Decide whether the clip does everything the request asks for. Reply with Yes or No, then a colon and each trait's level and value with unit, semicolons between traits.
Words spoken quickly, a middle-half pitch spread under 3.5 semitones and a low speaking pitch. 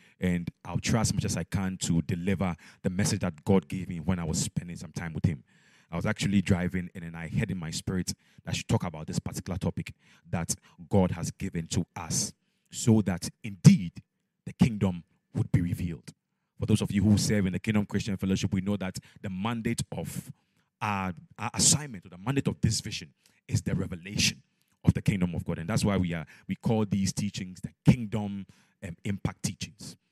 Yes: fast, 210 wpm; average, 2.9 semitones; very low, 95 Hz